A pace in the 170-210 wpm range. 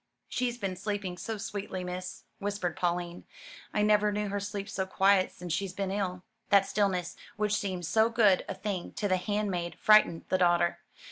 Yes: average, 180 wpm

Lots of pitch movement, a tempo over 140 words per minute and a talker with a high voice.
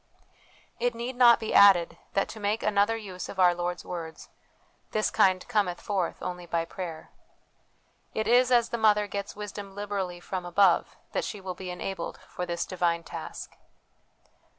No: average, 3.1 semitones; average, 170 wpm; high, 195 Hz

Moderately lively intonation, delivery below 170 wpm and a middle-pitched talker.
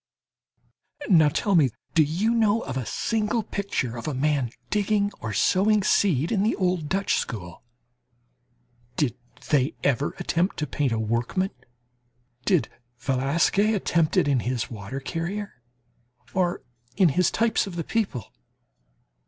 No: wide, 7.2 semitones; average, 140 wpm; medium, 165 Hz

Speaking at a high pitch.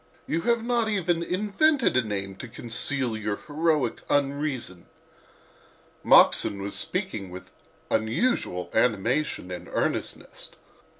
No: low, 135 Hz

